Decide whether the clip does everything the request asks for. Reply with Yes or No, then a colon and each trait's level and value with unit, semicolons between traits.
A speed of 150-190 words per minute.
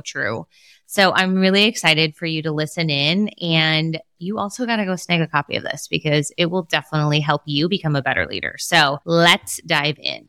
No: fast, 205 wpm